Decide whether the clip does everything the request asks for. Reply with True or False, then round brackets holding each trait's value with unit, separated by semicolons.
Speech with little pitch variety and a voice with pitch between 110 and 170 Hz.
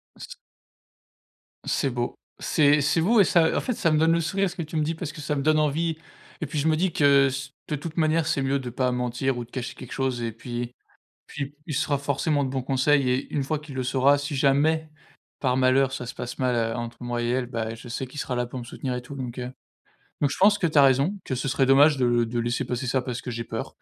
False (3.5 semitones; 135 Hz)